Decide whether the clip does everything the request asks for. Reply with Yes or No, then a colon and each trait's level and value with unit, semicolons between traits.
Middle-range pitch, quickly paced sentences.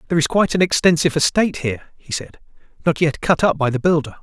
Yes: medium, 160 Hz; fast, 225 wpm